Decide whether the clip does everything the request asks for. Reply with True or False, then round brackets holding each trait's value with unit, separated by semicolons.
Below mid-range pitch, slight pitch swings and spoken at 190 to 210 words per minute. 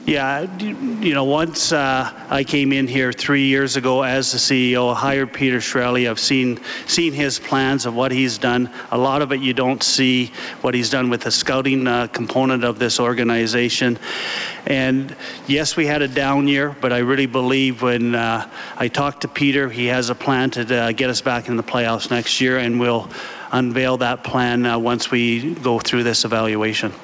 True (130 Hz; 2.1 semitones; 200 wpm)